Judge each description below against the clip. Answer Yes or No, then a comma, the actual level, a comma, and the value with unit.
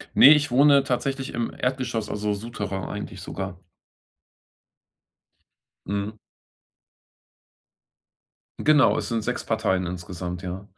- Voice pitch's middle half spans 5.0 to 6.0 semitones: Yes, wide, 5.4 semitones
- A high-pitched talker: No, low, 105 Hz